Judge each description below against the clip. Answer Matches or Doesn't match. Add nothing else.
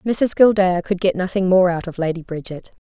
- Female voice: Matches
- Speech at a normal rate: Doesn't match